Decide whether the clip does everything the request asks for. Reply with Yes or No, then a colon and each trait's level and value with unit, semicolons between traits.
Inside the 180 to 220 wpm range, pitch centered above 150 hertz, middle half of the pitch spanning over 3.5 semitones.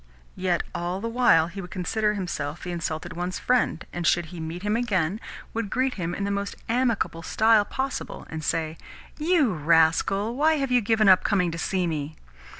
Yes: average, 190 wpm; medium, 185 Hz; average, 5.2 semitones